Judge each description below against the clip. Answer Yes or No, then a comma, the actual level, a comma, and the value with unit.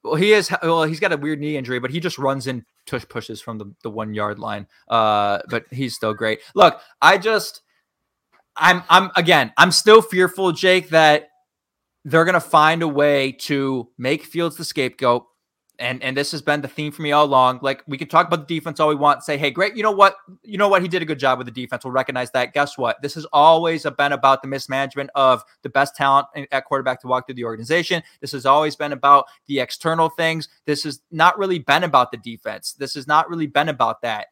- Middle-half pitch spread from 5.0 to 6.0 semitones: No, average, 3.9 semitones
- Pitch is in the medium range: Yes, medium, 145 Hz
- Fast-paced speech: Yes, fast, 235 wpm